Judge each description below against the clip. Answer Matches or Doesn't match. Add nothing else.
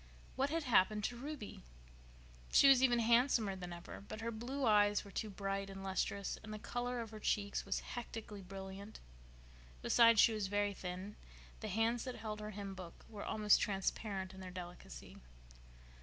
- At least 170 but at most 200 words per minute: Matches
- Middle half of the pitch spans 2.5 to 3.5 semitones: Matches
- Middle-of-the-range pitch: Doesn't match